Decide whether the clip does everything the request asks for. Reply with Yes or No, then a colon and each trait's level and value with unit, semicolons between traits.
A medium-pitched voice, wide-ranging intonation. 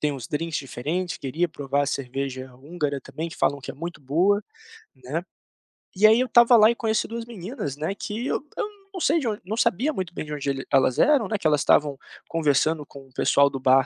Yes: medium, 160 Hz; wide, 7.5 semitones